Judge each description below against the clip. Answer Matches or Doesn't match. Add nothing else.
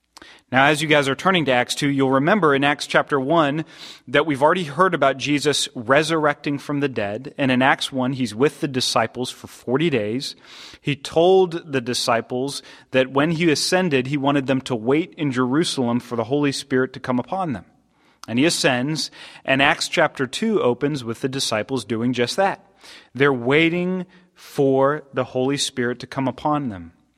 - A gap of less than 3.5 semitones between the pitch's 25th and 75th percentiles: Matches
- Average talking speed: Matches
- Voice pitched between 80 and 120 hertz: Doesn't match